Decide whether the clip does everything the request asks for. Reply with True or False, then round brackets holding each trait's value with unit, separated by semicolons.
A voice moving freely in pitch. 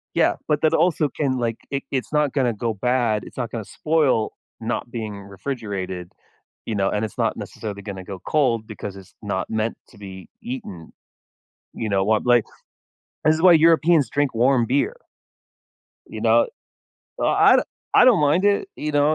True (6.1 semitones)